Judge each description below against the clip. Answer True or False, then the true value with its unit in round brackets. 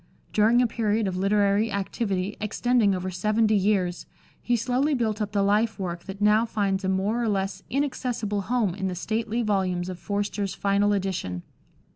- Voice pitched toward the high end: True (205 Hz)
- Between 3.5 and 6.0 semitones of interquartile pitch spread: False (2.6 semitones)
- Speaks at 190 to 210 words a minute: False (170 wpm)